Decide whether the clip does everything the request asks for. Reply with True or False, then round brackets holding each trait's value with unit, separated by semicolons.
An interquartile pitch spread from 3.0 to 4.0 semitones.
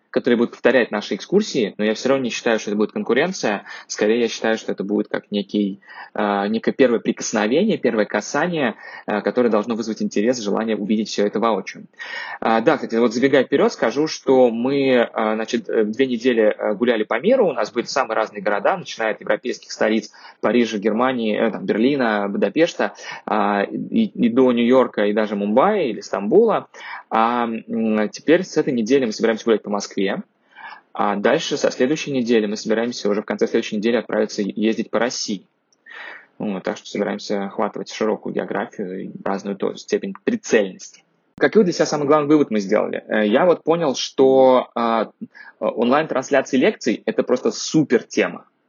True (3.4 semitones)